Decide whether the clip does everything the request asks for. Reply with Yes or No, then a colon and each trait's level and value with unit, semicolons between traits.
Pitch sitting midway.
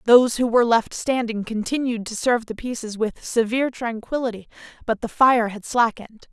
No: high, 230 Hz